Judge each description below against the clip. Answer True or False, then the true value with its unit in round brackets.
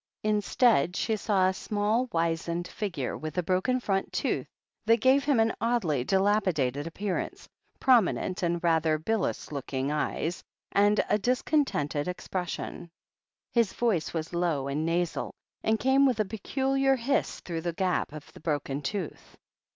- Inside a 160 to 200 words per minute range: False (150 wpm)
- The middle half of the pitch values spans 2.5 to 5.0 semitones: False (5.5 semitones)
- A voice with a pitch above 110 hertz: True (185 Hz)